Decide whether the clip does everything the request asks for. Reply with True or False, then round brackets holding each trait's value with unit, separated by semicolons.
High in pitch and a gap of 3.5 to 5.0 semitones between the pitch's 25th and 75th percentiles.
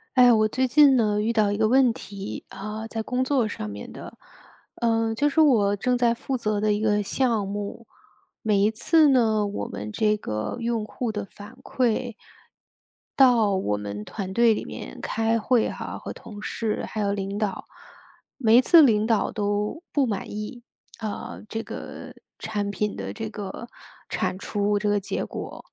False (215 Hz; 2.6 semitones)